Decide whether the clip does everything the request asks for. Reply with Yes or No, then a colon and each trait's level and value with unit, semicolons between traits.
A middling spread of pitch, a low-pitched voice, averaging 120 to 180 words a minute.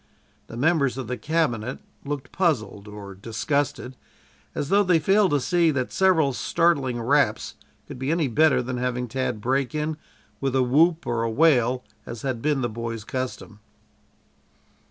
Yes: average, 4.6 semitones; low, 130 Hz; average, 160 wpm